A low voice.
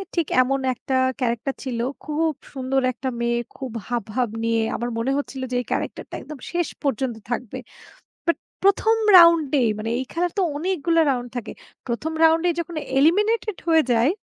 No: very high, 275 Hz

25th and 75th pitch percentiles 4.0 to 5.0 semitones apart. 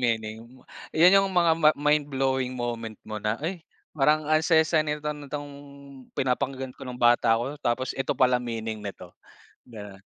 Yes: average, 4.5 semitones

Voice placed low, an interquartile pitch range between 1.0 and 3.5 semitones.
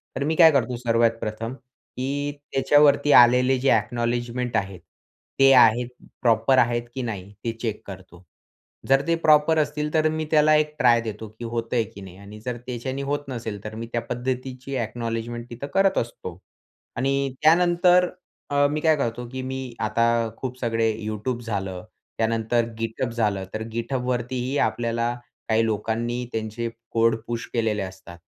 Yes: low, 120 Hz; average, 2.9 semitones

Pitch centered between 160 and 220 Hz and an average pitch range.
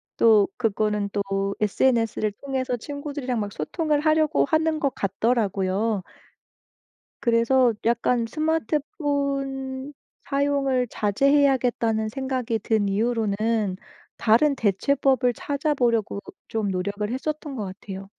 No: high, 240 Hz; average, 4.8 semitones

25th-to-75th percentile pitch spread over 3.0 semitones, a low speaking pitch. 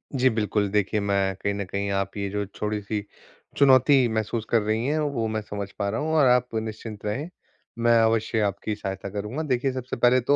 Yes: average, 3.5 semitones; low, 110 Hz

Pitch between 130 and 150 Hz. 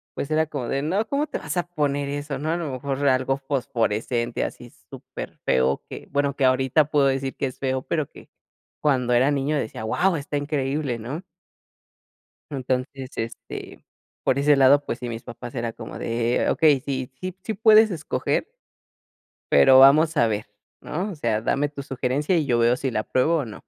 Yes: medium, 140 Hz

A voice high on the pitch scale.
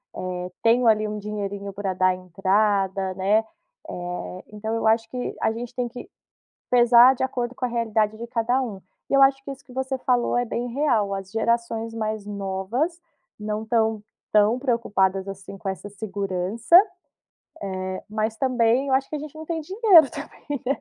Yes: high, 225 Hz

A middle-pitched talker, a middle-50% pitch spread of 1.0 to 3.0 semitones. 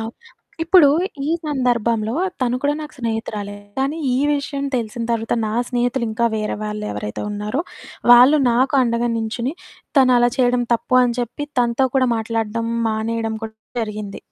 No: high, 235 Hz; narrow, 2.5 semitones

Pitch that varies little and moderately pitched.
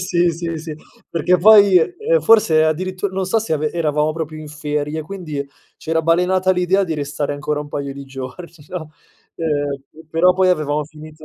No: average, 3.4 semitones; medium, 160 Hz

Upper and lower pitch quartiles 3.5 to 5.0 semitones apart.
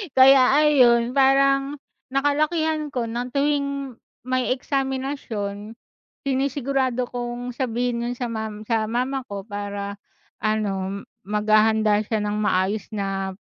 Yes: average, 4.2 semitones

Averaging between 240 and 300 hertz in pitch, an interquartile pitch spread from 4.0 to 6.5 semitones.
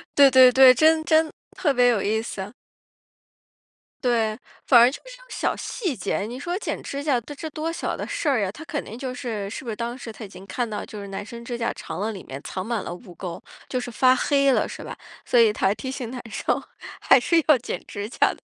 Yes: high, 245 Hz; average, 4.5 semitones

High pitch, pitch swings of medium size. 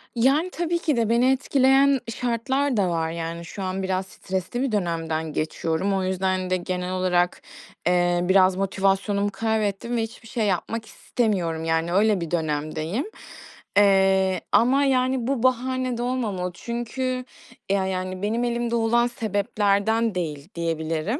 Yes: high, 200 Hz; average, 4.9 semitones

